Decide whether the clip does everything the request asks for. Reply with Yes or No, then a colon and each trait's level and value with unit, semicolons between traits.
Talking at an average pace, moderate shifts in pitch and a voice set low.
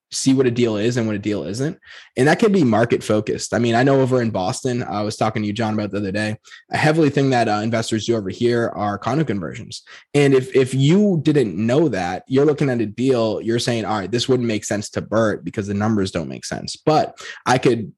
No: fast, 255 wpm; average, 3.9 semitones; low, 115 Hz